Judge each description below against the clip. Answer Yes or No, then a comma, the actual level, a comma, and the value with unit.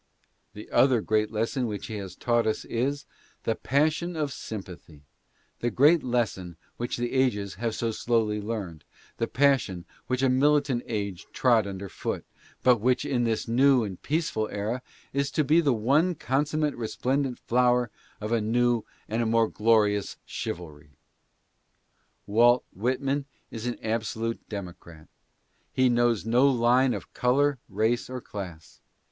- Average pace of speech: Yes, average, 150 wpm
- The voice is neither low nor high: No, low, 120 Hz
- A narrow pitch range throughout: No, average, 3.6 semitones